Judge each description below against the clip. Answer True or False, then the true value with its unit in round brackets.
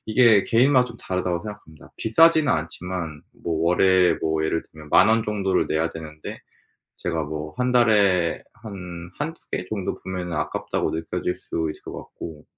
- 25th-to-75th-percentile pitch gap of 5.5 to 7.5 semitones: False (5.1 semitones)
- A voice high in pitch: False (90 Hz)